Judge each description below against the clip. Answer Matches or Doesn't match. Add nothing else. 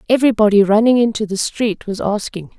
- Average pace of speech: Matches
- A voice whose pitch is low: Doesn't match